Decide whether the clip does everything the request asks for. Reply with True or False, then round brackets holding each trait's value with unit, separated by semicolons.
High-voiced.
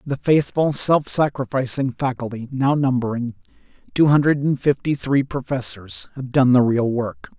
False (130 Hz)